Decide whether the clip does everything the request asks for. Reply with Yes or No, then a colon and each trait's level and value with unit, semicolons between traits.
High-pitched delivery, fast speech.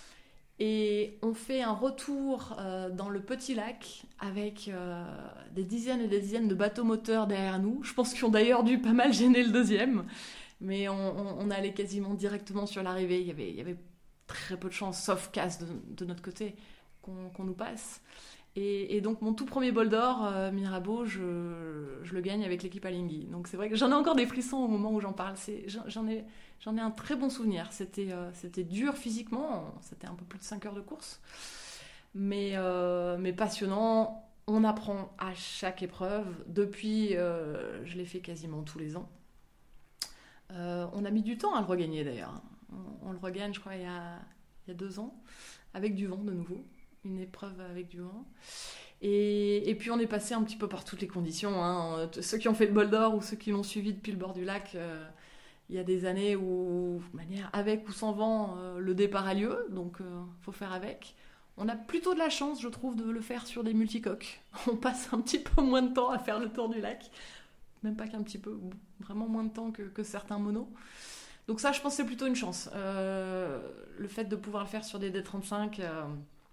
Yes: high, 205 Hz; fast, 225 wpm